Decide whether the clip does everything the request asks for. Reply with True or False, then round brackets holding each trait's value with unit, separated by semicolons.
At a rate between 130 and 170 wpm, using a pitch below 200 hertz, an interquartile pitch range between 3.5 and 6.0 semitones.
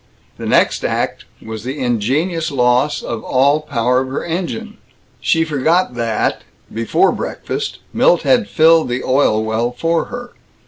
True (145 wpm; 140 Hz; 5.4 semitones)